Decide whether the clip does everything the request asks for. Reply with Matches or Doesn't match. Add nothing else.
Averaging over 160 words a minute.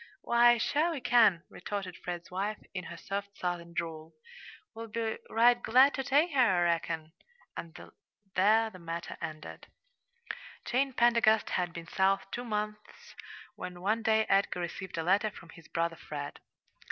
Doesn't match